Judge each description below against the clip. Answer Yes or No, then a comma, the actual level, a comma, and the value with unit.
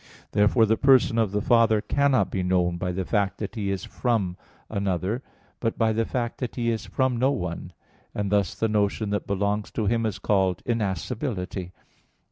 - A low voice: Yes, low, 105 Hz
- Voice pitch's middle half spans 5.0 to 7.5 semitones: No, average, 3.2 semitones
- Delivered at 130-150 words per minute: No, average, 185 wpm